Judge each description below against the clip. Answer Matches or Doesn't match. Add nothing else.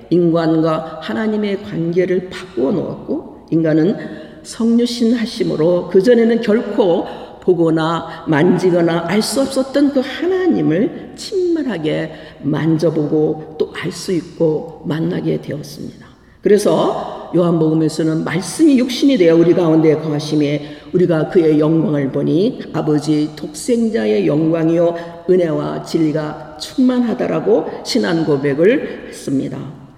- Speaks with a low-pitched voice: Doesn't match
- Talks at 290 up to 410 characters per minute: Doesn't match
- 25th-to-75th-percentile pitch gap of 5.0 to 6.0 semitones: Matches